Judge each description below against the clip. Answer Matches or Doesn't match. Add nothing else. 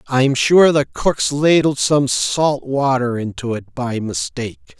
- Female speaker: Doesn't match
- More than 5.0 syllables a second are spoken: Doesn't match